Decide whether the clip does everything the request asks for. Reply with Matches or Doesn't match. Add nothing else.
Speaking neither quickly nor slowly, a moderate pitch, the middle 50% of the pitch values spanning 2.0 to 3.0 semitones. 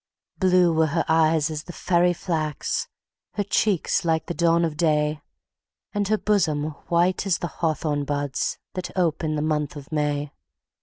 Matches